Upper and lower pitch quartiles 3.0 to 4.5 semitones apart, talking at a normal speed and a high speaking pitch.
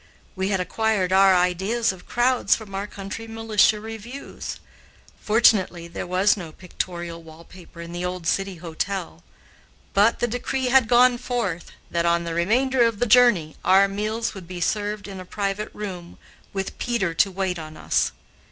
Yes: average, 4.0 semitones; average, 170 wpm; high, 195 Hz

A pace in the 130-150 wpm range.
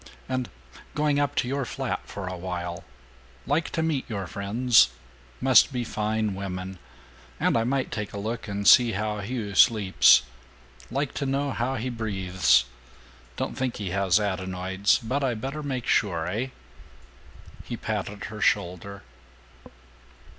Yes: average, 145 wpm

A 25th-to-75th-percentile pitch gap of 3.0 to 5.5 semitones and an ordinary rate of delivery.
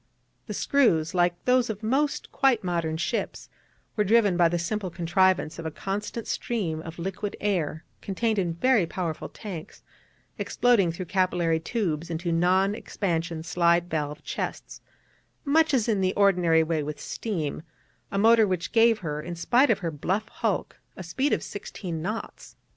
Yes: average, 4.5 semitones; average, 160 wpm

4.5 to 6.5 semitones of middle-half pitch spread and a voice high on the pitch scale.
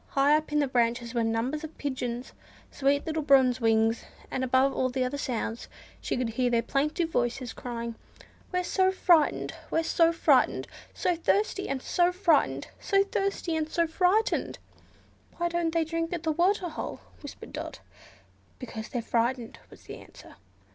Yes: wide, 5.4 semitones; very high, 285 Hz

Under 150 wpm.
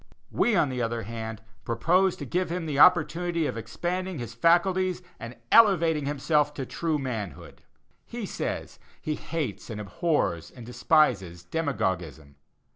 Yes: average, 140 wpm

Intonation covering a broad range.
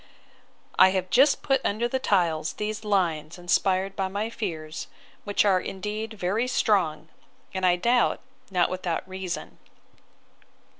No: average, 3.1 semitones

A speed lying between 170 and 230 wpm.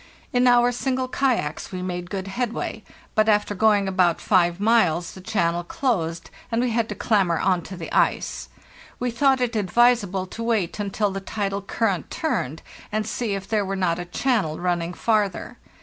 Yes: average, 180 wpm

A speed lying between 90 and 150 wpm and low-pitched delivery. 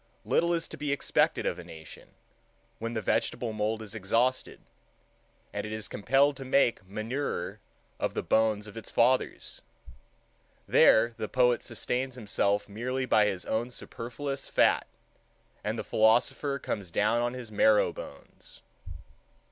Yes: average, 145 wpm; low, 115 Hz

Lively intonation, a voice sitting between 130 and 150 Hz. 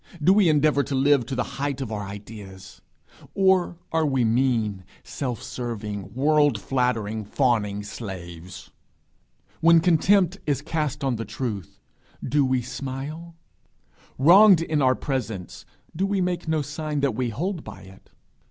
Yes: wide, 6.0 semitones; low, 135 Hz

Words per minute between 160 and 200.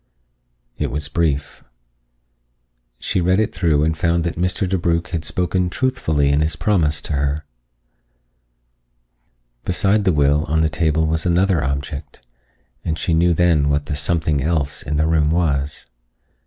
No: average, 150 wpm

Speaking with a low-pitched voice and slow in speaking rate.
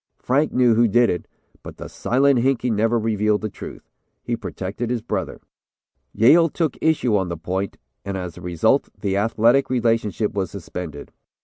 No: low, 110 Hz; average, 175 wpm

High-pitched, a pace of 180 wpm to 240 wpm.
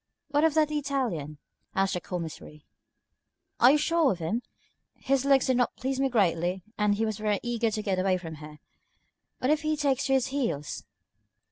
Yes: high, 235 Hz; average, 190 wpm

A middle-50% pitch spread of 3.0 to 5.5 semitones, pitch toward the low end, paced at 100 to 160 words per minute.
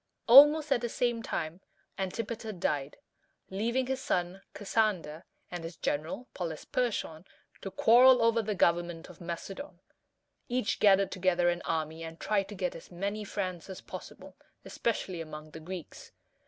No: average, 5.2 semitones; high, 190 Hz; average, 155 wpm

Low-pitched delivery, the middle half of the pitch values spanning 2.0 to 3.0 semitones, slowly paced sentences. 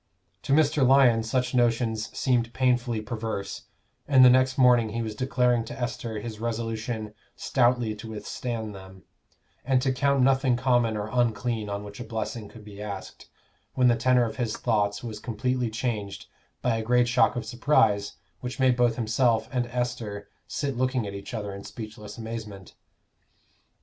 No: low, 115 Hz; narrow, 2.6 semitones; average, 165 wpm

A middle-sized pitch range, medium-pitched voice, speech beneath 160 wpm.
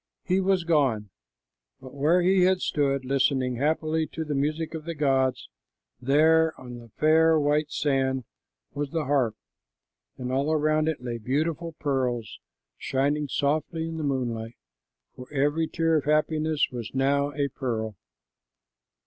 Yes: average, 3.2 semitones; medium, 145 Hz; average, 145 wpm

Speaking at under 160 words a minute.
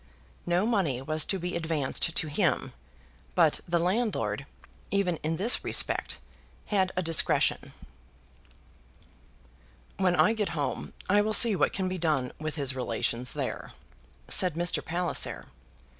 Yes: slow, 135 wpm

